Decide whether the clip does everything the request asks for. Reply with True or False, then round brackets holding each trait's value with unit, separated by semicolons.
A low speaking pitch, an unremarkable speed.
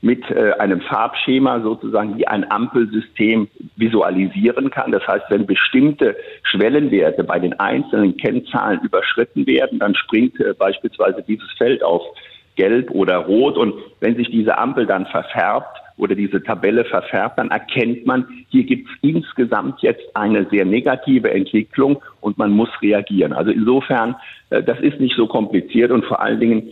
True (130 Hz; 150 wpm)